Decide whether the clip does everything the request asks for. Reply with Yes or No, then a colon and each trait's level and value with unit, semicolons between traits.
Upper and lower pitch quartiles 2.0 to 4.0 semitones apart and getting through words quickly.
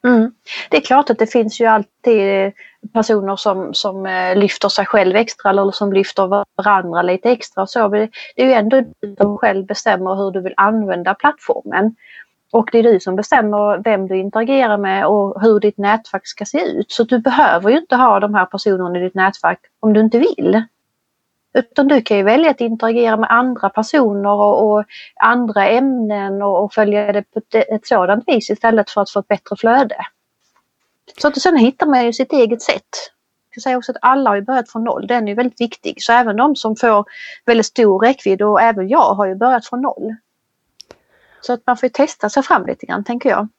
Yes: average, 3.4 semitones; fast, 200 wpm